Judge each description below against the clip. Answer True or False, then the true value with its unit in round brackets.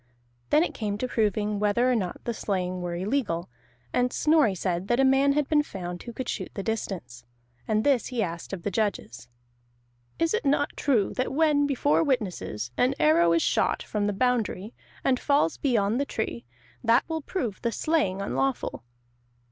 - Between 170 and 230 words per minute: True (180 wpm)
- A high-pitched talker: True (220 Hz)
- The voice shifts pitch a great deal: True (6.6 semitones)